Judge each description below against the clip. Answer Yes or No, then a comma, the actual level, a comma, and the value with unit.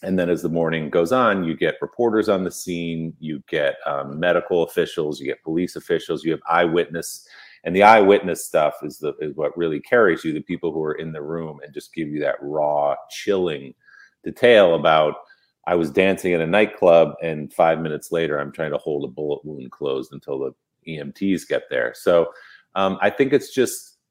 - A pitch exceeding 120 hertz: No, very low, 90 Hz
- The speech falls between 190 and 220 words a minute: Yes, average, 200 wpm